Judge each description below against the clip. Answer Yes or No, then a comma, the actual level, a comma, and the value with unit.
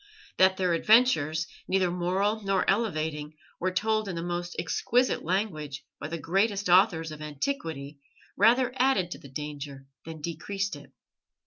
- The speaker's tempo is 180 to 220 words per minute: No, average, 145 wpm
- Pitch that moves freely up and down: No, average, 4.6 semitones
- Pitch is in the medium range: Yes, medium, 175 Hz